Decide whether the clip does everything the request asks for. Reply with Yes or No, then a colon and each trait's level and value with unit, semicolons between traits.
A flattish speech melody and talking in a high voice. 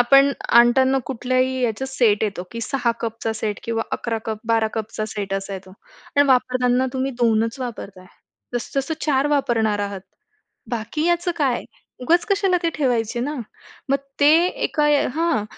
No: average, 3.6 semitones; high, 245 Hz